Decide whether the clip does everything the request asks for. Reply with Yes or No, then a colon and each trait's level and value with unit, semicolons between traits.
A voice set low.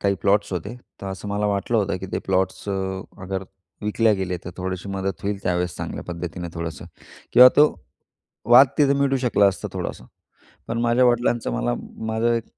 Yes: low, 100 Hz